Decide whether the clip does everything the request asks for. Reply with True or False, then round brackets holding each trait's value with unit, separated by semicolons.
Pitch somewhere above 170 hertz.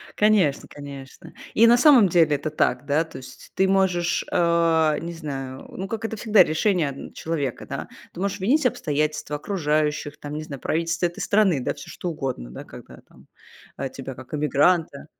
False (160 Hz)